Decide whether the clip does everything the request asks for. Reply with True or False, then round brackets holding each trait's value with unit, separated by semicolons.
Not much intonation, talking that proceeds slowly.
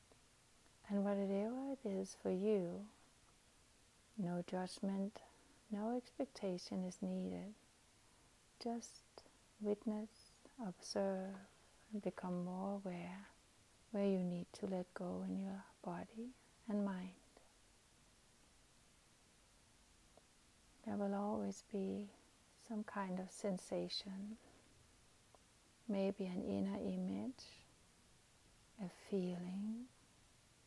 True (2.3 semitones; 85 wpm)